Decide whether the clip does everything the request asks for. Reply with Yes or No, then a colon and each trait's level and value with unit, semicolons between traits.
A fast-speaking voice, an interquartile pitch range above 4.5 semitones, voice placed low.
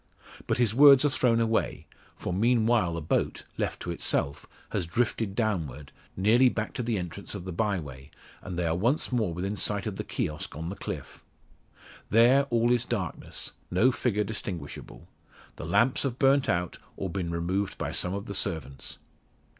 No: average, 180 wpm; wide, 5.4 semitones; low, 100 Hz